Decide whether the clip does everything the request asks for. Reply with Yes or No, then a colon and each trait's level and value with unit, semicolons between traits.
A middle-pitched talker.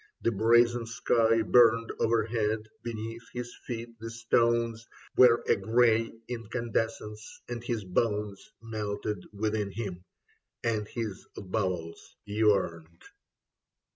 No: low, 115 Hz